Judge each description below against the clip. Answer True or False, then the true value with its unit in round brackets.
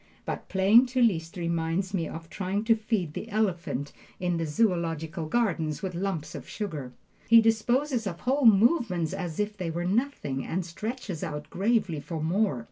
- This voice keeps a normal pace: True (170 wpm)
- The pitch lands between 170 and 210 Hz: True (185 Hz)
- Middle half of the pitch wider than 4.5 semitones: True (5.1 semitones)